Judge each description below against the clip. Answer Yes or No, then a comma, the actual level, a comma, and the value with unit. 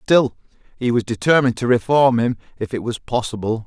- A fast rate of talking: No, average, 180 wpm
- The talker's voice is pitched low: Yes, low, 120 Hz